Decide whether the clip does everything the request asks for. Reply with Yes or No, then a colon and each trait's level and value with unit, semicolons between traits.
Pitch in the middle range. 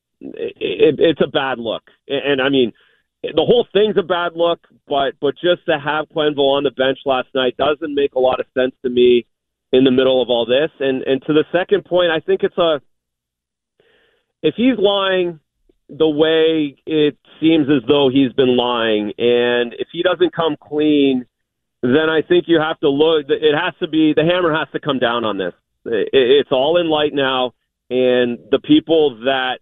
Yes: medium, 150 Hz